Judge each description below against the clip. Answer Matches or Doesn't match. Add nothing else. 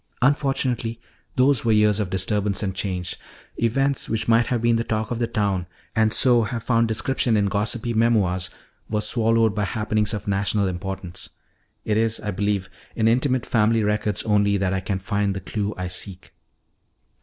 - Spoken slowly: Doesn't match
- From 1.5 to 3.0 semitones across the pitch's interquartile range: Matches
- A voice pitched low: Matches